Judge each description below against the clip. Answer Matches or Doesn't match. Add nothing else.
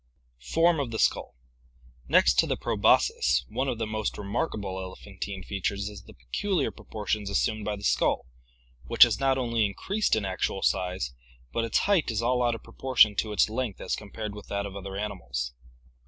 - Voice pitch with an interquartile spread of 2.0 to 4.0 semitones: Matches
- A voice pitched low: Matches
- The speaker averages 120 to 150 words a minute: Doesn't match